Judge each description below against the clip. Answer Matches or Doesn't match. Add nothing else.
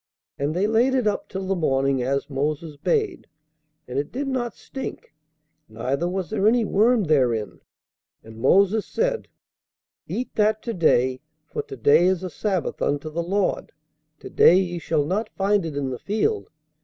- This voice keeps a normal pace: Matches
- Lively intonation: Matches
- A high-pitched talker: Doesn't match